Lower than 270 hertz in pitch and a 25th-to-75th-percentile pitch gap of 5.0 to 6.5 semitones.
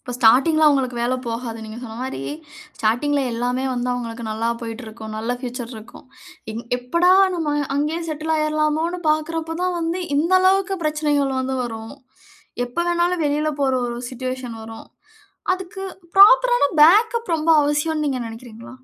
No: very high, 280 Hz; average, 5.3 semitones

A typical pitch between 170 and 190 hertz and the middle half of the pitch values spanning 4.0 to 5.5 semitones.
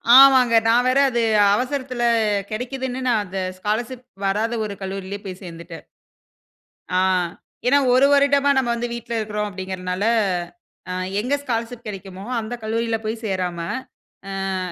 No: high, 225 Hz; average, 4.3 semitones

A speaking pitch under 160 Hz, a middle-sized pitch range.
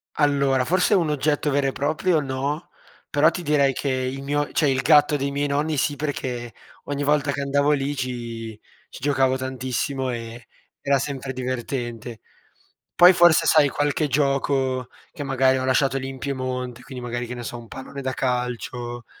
No: low, 135 Hz; narrow, 2.3 semitones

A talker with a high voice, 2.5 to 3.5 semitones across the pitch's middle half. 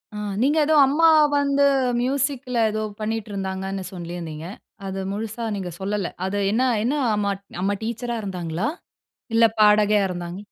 No: high, 210 Hz; average, 4.2 semitones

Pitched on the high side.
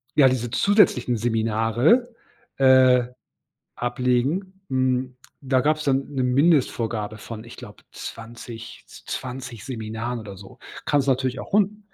No: low, 125 Hz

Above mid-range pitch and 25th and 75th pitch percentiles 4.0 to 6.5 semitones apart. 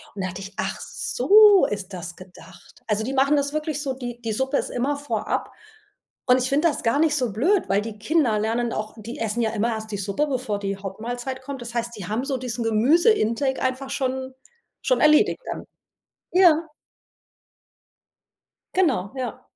Yes: high, 245 Hz; average, 4.8 semitones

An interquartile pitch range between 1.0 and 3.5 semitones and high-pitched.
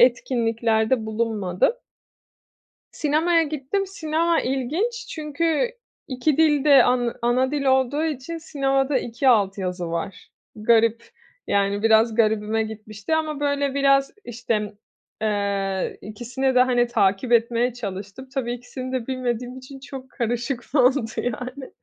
No: average, 4.0 semitones; very high, 250 Hz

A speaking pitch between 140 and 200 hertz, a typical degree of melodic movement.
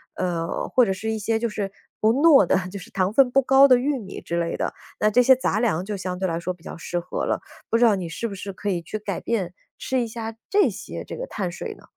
No: high, 210 Hz; average, 4.6 semitones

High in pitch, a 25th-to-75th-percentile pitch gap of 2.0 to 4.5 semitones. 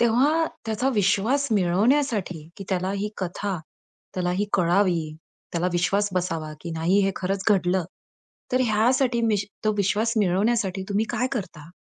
Yes: high, 200 Hz; average, 3.7 semitones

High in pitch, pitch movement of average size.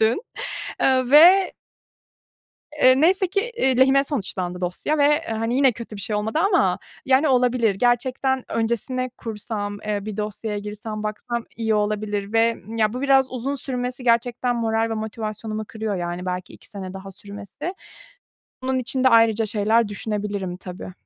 Yes: high, 225 Hz; average, 3.6 semitones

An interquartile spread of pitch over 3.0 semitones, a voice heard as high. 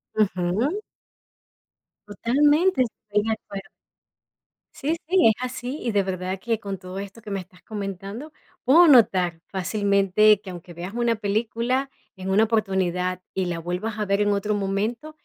Yes: average, 3.7 semitones; high, 205 Hz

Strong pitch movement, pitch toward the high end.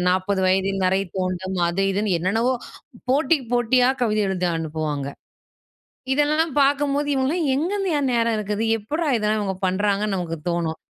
Yes: wide, 6.5 semitones; high, 210 Hz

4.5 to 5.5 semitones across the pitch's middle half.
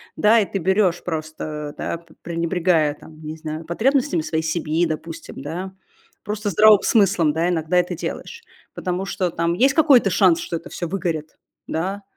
No: average, 3.5 semitones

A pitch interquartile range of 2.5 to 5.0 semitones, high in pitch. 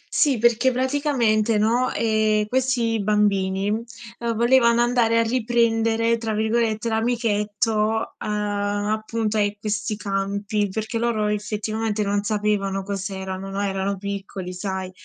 No: narrow, 2.1 semitones; high, 215 Hz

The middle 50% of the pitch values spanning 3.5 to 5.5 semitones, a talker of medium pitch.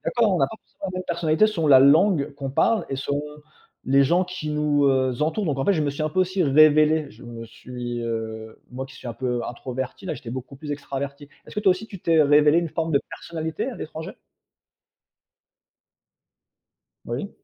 Yes: average, 4.2 semitones; medium, 150 Hz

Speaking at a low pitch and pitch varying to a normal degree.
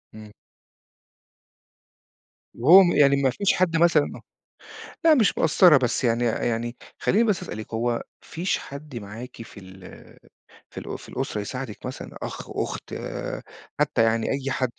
No: low, 130 Hz; wide, 6.5 semitones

